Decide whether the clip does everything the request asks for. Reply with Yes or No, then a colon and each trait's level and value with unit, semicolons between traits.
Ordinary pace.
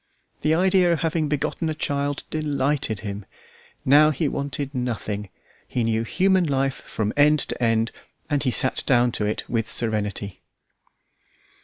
Yes: average, 150 wpm